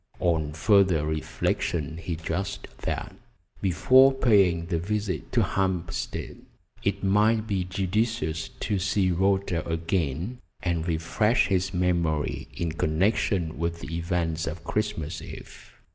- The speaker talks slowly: Yes, slow, 120 wpm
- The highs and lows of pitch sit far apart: No, average, 3.3 semitones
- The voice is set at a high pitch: No, very low, 90 Hz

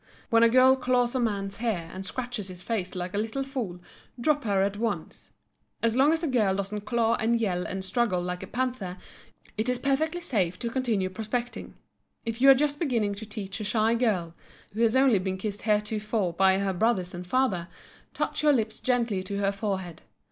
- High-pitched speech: Yes, high, 220 Hz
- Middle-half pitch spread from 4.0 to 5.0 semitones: Yes, average, 4.3 semitones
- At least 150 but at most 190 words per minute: No, average, 200 wpm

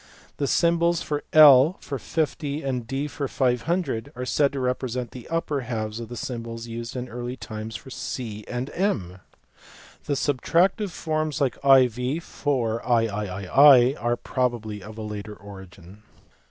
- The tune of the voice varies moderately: Yes, average, 4.2 semitones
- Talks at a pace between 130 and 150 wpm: Yes, average, 145 wpm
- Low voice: Yes, low, 125 Hz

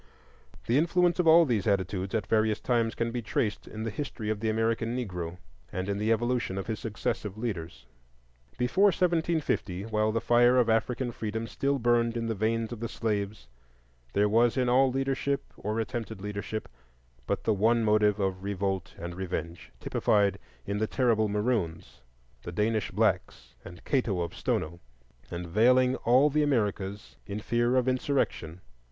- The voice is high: No, low, 110 Hz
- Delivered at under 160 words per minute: No, average, 165 wpm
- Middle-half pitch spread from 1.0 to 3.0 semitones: No, average, 3.4 semitones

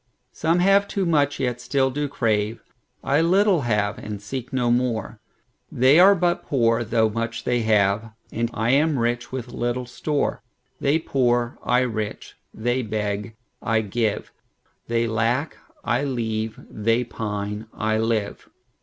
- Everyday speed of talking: No, slow, 130 wpm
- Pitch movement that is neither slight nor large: Yes, average, 3.5 semitones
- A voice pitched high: No, low, 120 Hz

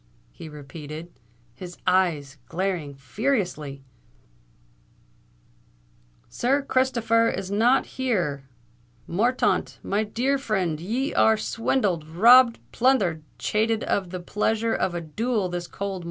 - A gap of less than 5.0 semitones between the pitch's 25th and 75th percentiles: No, wide, 5.6 semitones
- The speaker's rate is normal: No, slow, 100 wpm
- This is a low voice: No, high, 195 Hz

